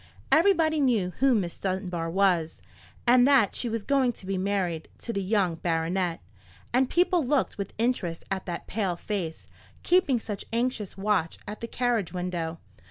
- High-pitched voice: Yes, high, 200 Hz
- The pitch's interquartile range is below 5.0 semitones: No, wide, 5.6 semitones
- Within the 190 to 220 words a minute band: No, average, 165 wpm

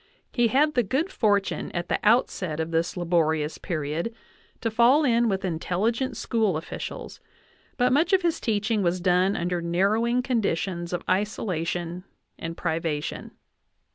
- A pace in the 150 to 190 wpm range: No, average, 140 wpm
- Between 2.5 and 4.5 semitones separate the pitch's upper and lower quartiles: No, wide, 5.5 semitones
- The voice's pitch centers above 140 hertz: Yes, high, 190 Hz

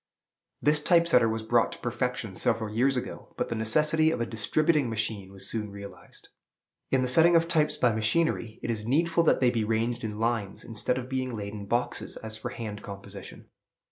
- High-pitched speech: No, low, 115 Hz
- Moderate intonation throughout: Yes, average, 4.1 semitones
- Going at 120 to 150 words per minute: No, average, 200 wpm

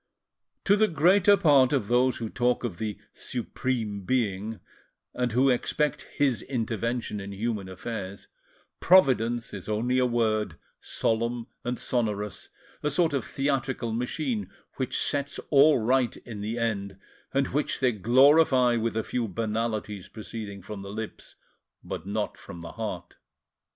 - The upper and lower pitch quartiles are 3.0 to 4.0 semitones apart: Yes, average, 3.6 semitones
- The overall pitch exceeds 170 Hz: No, low, 115 Hz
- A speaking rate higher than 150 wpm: No, average, 145 wpm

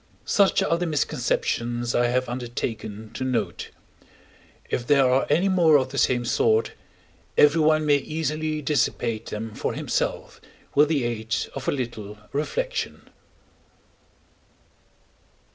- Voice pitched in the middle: No, low, 130 Hz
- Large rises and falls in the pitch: No, average, 4.5 semitones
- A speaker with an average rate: No, slow, 125 wpm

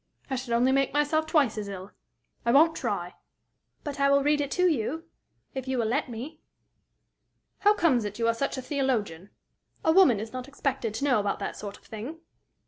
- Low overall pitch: No, very high, 260 Hz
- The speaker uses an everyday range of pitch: Yes, average, 4.7 semitones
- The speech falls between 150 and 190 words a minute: No, average, 200 wpm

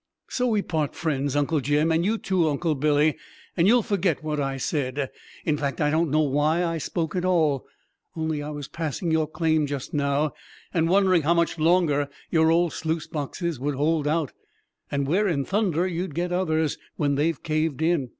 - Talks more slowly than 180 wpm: No, average, 190 wpm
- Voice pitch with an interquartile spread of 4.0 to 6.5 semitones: No, average, 2.7 semitones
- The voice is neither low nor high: Yes, medium, 155 Hz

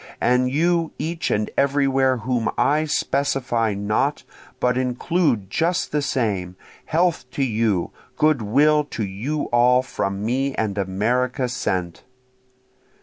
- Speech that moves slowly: Yes, slow, 125 wpm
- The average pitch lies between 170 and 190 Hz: No, low, 125 Hz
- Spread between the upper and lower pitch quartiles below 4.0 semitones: No, average, 5.0 semitones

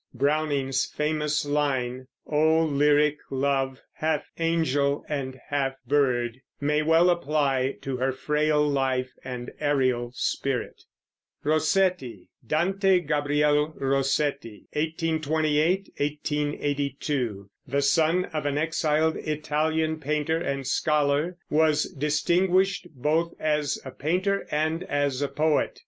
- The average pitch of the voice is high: No, medium, 150 Hz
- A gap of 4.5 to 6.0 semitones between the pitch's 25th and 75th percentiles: No, narrow, 2.4 semitones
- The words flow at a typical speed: No, slow, 105 wpm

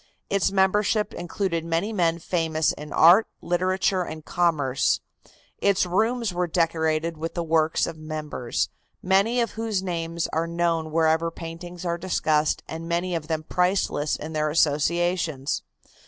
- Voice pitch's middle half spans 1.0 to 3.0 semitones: Yes, narrow, 2.6 semitones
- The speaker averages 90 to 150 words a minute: Yes, average, 140 wpm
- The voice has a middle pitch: Yes, medium, 170 Hz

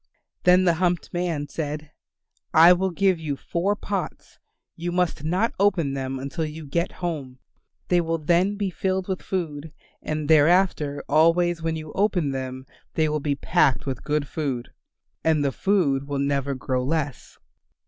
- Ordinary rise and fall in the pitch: Yes, average, 3.8 semitones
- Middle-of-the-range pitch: Yes, medium, 160 Hz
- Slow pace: No, average, 160 wpm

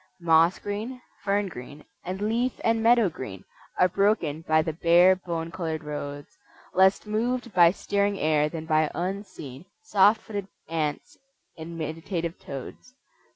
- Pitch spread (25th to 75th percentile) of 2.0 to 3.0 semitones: No, average, 4.4 semitones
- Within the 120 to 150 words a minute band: Yes, average, 140 wpm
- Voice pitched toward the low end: No, medium, 175 Hz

